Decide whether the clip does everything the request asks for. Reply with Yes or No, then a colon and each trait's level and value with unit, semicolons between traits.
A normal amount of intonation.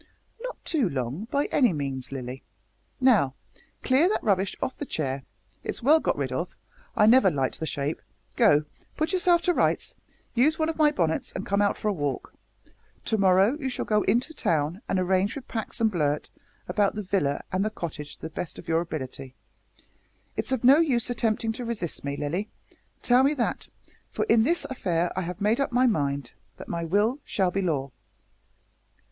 No: wide, 8.2 semitones